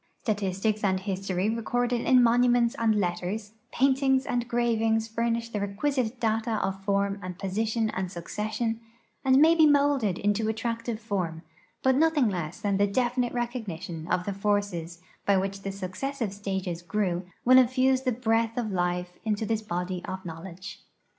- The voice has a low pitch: No, high, 215 Hz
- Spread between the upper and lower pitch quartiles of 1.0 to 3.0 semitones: No, average, 4.0 semitones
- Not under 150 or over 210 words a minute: Yes, average, 160 wpm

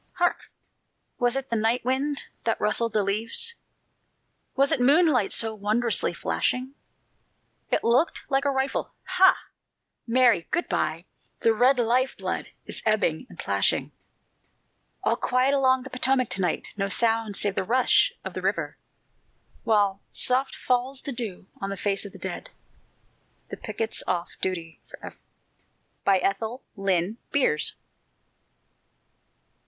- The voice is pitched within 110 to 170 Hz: No, high, 235 Hz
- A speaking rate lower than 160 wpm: Yes, slow, 135 wpm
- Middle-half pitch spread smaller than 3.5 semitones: No, average, 4.5 semitones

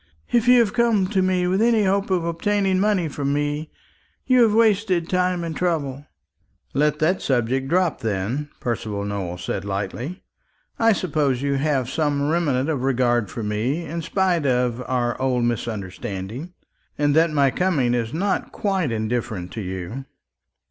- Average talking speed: Yes, average, 160 wpm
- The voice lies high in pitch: No, medium, 145 Hz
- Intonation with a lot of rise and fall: Yes, wide, 7.1 semitones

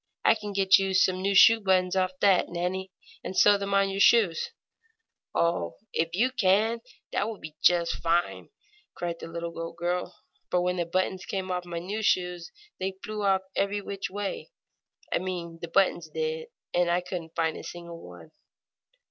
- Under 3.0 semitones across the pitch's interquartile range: Yes, narrow, 2.6 semitones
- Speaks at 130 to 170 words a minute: No, average, 180 wpm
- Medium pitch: Yes, medium, 180 Hz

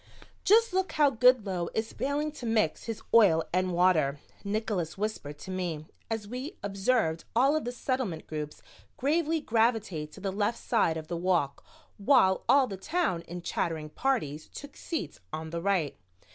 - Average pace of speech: Yes, average, 165 wpm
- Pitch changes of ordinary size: No, wide, 7.2 semitones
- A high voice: Yes, high, 200 Hz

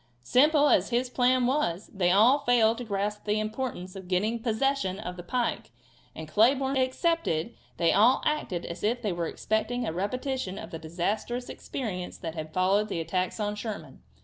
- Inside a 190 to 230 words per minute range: No, average, 175 wpm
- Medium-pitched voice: No, high, 215 Hz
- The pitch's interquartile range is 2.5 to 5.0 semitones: No, wide, 5.4 semitones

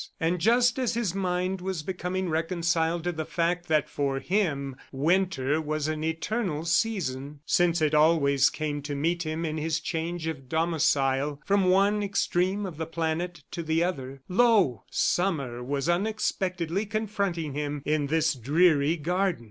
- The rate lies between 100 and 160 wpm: Yes, average, 155 wpm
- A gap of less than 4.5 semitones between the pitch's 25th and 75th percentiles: Yes, average, 3.5 semitones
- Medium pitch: Yes, medium, 165 Hz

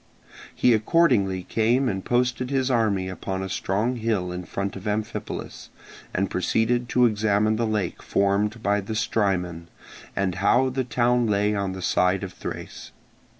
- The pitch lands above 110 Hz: No, low, 105 Hz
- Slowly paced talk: No, average, 155 wpm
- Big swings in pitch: No, average, 3.7 semitones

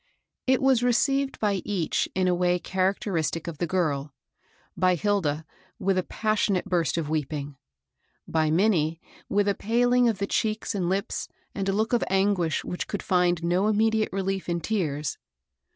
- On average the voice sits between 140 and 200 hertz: Yes, high, 190 Hz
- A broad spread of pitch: No, average, 3.9 semitones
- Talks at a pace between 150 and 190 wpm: Yes, average, 170 wpm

